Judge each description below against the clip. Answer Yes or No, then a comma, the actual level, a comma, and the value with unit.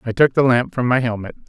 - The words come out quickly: Yes, fast, 285 wpm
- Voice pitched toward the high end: No, low, 125 Hz